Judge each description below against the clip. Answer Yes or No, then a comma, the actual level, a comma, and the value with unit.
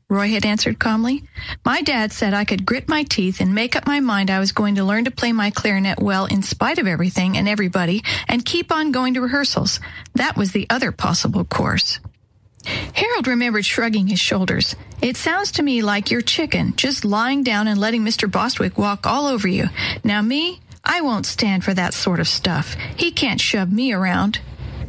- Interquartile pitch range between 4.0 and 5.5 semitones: Yes, average, 4.3 semitones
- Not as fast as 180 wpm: No, average, 200 wpm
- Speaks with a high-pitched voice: Yes, high, 220 Hz